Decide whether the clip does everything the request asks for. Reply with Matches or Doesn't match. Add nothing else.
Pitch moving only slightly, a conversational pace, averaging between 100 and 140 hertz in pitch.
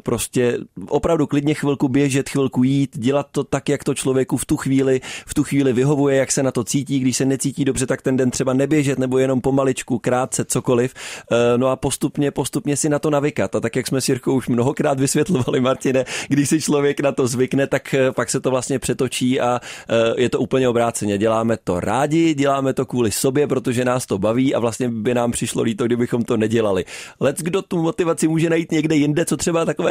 Doesn't match